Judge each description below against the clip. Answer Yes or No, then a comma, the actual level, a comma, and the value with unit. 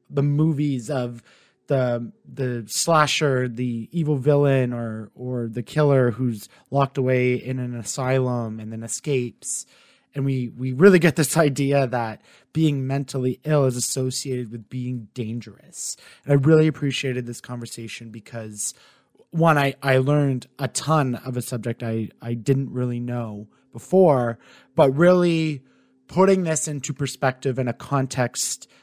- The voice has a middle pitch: No, low, 130 Hz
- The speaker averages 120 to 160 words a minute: Yes, average, 145 wpm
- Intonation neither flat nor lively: Yes, average, 3.2 semitones